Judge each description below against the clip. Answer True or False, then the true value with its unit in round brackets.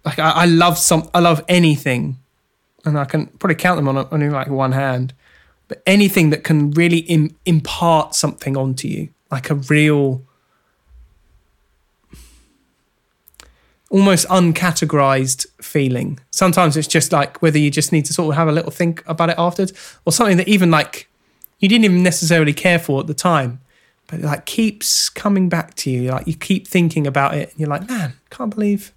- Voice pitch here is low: False (155 Hz)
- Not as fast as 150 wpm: False (180 wpm)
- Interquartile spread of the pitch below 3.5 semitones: False (4.0 semitones)